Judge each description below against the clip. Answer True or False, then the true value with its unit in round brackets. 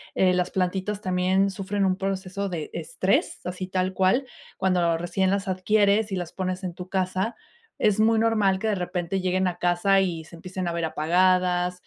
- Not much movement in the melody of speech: True (1.4 semitones)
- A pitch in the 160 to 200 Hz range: True (185 Hz)